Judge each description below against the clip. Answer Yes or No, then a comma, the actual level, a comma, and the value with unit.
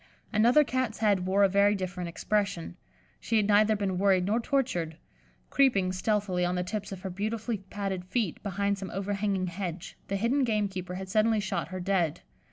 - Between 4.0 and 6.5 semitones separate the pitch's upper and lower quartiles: No, narrow, 2.5 semitones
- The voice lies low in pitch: No, high, 200 Hz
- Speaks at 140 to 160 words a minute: No, average, 175 wpm